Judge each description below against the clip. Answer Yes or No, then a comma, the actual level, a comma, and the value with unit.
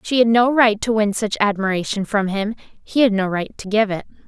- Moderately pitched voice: No, high, 210 Hz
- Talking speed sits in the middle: No, fast, 225 wpm